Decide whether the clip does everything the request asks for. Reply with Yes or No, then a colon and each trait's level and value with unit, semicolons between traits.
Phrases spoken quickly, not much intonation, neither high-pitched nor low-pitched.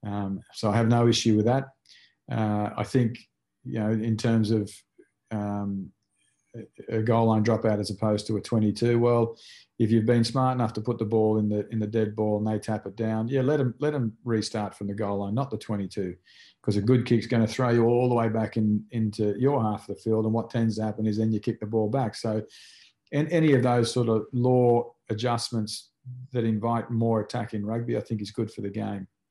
No: fast, 230 wpm; narrow, 1.9 semitones; low, 110 Hz